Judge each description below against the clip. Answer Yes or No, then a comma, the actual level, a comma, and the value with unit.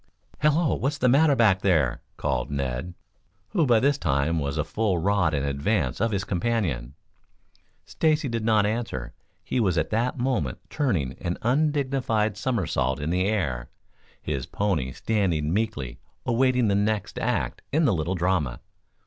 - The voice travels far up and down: Yes, wide, 7.9 semitones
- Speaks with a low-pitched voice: Yes, low, 100 Hz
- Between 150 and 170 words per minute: Yes, average, 155 wpm